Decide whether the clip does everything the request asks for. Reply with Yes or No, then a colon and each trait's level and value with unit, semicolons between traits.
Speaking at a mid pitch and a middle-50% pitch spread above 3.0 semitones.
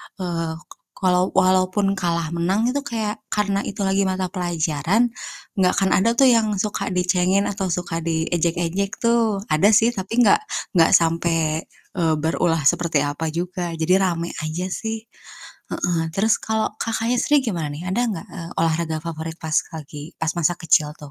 Yes: medium, 180 Hz; average, 3.5 semitones